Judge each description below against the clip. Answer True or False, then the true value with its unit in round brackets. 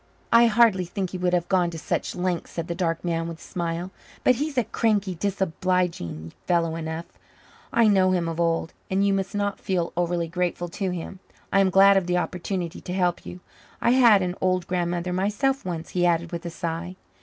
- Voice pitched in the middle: True (180 Hz)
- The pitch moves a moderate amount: False (2.3 semitones)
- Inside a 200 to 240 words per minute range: True (205 wpm)